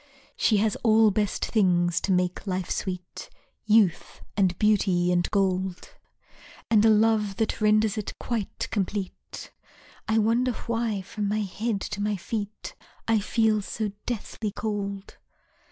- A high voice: Yes, high, 210 Hz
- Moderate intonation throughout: No, narrow, 2.3 semitones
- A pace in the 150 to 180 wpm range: No, slow, 135 wpm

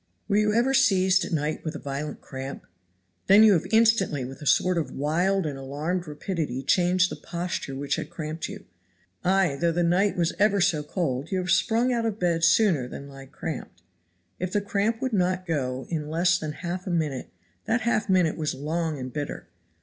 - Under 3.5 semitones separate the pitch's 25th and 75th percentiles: No, average, 4.6 semitones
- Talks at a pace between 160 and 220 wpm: Yes, average, 200 wpm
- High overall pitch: No, medium, 170 Hz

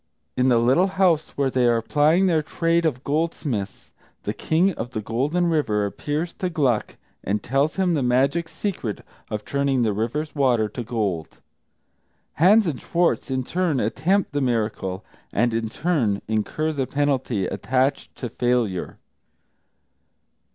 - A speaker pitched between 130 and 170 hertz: Yes, low, 135 Hz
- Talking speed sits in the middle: Yes, average, 150 wpm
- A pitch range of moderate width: No, wide, 5.9 semitones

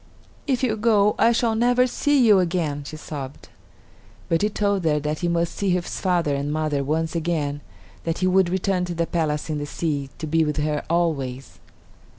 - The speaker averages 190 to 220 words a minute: Yes, average, 195 wpm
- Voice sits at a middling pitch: Yes, medium, 170 Hz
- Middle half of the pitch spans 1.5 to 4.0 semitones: No, average, 4.6 semitones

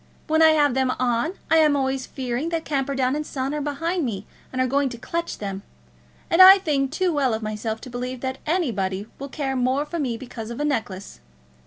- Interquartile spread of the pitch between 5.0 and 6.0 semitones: No, average, 3.8 semitones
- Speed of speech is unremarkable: No, fast, 215 wpm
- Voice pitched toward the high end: Yes, very high, 265 Hz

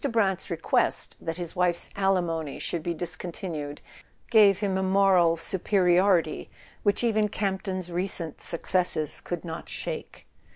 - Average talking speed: No, slow, 125 wpm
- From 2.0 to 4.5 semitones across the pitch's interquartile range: Yes, narrow, 2.6 semitones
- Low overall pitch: No, medium, 180 Hz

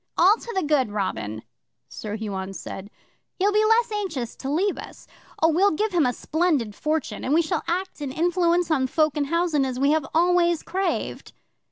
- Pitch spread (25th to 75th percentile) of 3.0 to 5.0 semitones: No, wide, 5.4 semitones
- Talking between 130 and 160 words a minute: No, average, 195 wpm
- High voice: Yes, very high, 315 Hz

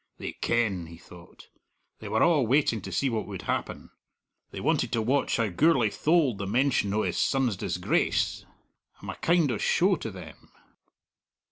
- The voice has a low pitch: Yes, low, 115 Hz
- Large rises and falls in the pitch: Yes, wide, 6.0 semitones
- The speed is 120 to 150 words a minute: No, average, 170 wpm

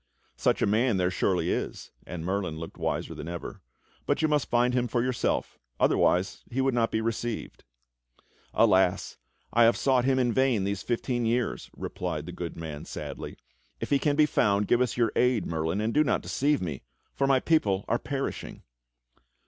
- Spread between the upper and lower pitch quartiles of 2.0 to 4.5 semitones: No, average, 4.9 semitones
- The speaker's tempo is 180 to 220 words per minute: Yes, average, 185 wpm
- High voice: No, low, 120 Hz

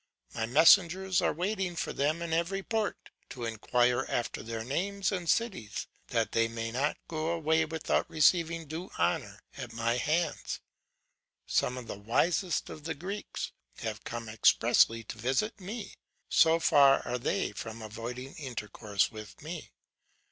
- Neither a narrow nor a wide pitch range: No, wide, 6.9 semitones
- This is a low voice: No, medium, 150 Hz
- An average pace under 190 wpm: Yes, average, 150 wpm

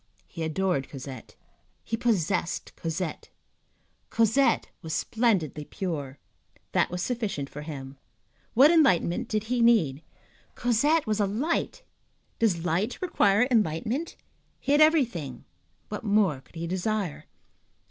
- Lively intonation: Yes, wide, 6.8 semitones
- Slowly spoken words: Yes, slow, 120 wpm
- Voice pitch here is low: No, high, 200 Hz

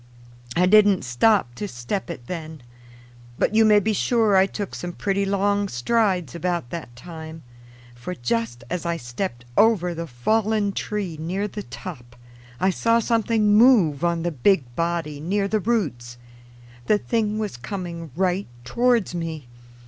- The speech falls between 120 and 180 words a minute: Yes, average, 155 wpm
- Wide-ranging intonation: No, average, 4.8 semitones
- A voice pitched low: No, medium, 180 Hz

